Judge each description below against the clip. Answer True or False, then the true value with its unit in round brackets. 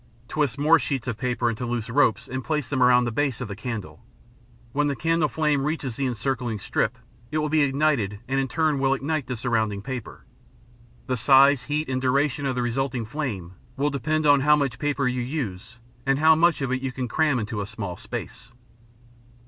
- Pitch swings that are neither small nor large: True (3.5 semitones)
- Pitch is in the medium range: False (130 Hz)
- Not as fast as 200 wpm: False (205 wpm)